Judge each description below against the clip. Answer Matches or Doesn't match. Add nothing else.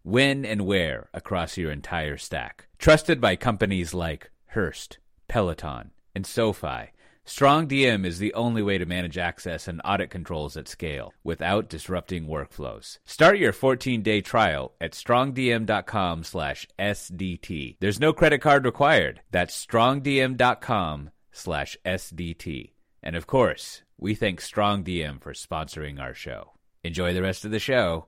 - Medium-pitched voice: Doesn't match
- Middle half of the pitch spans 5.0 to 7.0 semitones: Matches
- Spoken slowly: Matches